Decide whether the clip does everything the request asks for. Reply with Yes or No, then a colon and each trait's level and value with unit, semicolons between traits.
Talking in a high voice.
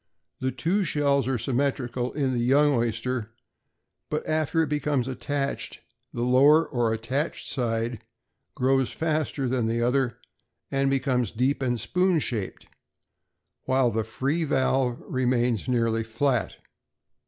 No: low, 130 Hz